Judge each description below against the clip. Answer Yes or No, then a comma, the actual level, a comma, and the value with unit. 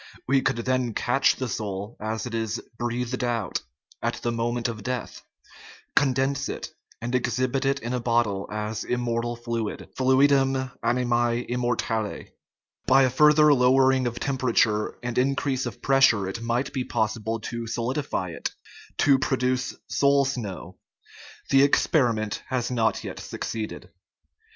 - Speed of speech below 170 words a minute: Yes, average, 150 wpm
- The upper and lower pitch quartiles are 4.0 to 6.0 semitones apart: No, narrow, 2.5 semitones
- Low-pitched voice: Yes, low, 120 Hz